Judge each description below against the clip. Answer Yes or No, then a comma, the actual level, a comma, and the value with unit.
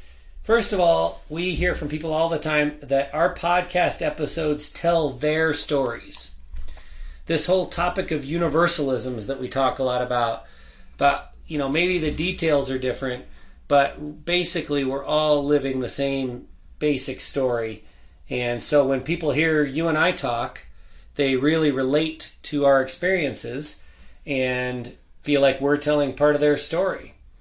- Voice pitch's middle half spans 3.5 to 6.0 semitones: Yes, average, 4.0 semitones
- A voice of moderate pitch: Yes, medium, 145 Hz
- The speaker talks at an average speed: Yes, average, 150 wpm